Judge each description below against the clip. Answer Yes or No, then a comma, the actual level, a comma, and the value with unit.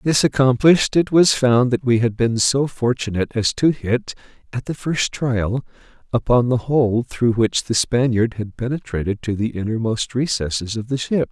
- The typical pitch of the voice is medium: No, low, 120 Hz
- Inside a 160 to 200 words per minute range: Yes, average, 180 wpm